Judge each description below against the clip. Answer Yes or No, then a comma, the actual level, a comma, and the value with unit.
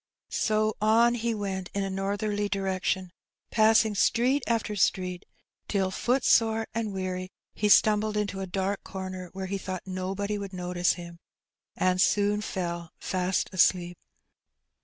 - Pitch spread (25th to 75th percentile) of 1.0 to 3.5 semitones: Yes, narrow, 2.4 semitones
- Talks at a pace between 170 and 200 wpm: No, slow, 135 wpm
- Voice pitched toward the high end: Yes, high, 195 Hz